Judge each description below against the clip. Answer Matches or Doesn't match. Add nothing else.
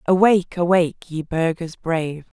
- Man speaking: Doesn't match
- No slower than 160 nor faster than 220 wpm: Doesn't match